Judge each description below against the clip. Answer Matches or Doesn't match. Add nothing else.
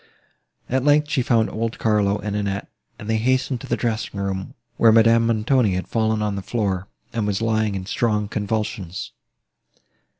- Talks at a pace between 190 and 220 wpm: Doesn't match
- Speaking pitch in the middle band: Doesn't match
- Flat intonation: Matches